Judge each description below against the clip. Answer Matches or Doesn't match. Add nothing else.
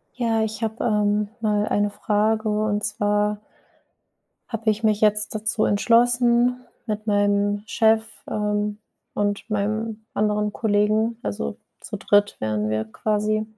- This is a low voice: Doesn't match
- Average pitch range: Doesn't match